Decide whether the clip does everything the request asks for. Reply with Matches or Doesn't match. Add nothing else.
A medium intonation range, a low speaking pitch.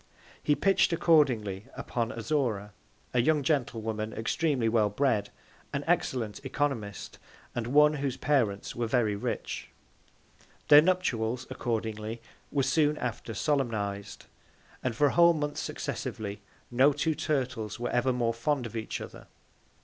Matches